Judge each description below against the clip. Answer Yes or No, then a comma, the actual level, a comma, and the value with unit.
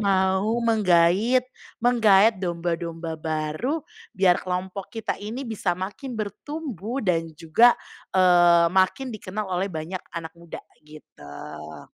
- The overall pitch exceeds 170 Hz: Yes, medium, 185 Hz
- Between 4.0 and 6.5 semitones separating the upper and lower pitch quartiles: Yes, average, 4.6 semitones